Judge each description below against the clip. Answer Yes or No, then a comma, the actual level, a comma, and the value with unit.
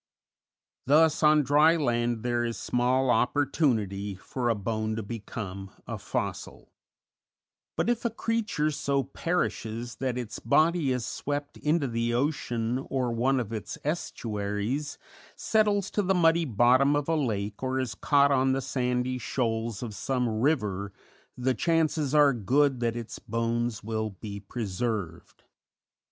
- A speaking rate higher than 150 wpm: No, average, 140 wpm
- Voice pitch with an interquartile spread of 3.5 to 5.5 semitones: Yes, average, 4.4 semitones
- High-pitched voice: No, low, 125 Hz